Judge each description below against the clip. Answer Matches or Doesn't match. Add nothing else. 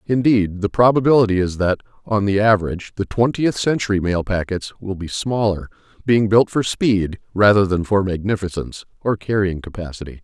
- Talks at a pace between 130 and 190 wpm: Matches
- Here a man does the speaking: Matches